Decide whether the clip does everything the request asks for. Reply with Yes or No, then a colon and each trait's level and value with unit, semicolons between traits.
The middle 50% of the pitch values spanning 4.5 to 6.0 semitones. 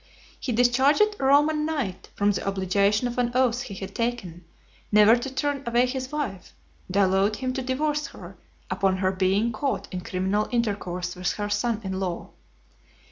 Yes: average, 5.2 semitones